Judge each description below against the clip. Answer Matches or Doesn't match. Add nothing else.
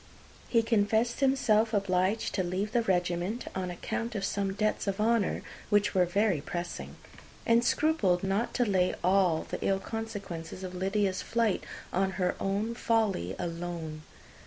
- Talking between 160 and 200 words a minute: Doesn't match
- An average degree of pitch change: Matches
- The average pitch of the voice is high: Matches